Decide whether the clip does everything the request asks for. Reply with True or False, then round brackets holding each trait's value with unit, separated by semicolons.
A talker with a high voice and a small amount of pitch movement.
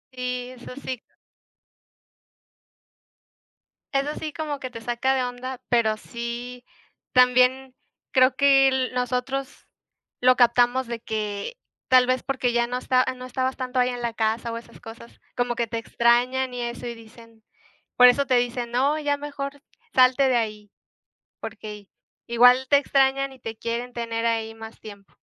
True (250 Hz; 1.8 semitones)